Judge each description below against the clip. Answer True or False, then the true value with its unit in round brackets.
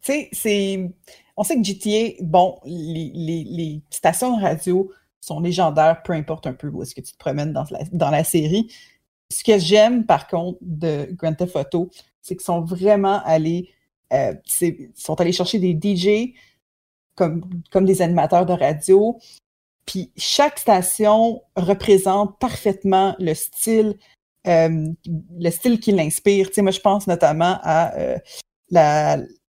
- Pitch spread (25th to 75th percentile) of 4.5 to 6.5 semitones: False (3.6 semitones)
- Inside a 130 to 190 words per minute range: True (160 wpm)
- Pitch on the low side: False (180 Hz)